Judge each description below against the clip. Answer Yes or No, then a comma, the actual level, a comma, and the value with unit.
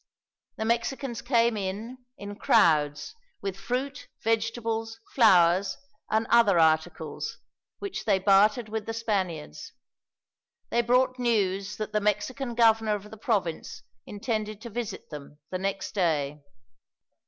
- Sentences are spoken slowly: Yes, slow, 125 wpm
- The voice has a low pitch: No, high, 215 Hz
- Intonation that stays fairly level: No, average, 3.5 semitones